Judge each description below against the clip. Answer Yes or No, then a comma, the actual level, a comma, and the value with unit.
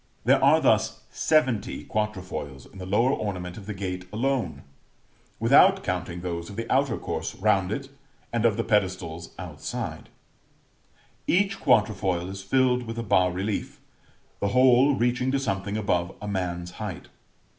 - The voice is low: Yes, low, 105 Hz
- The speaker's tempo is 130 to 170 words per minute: Yes, average, 150 wpm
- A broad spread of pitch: No, average, 4.8 semitones